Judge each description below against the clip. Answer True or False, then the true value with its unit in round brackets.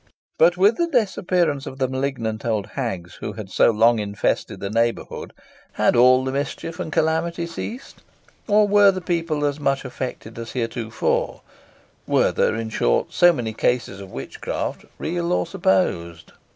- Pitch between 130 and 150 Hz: True (135 Hz)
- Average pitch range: False (7.3 semitones)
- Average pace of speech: True (150 wpm)